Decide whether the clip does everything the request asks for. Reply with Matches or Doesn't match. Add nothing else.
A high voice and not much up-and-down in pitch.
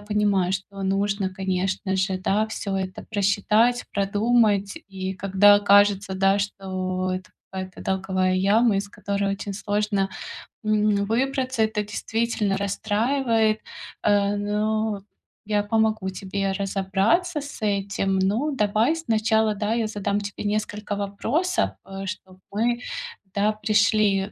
Matches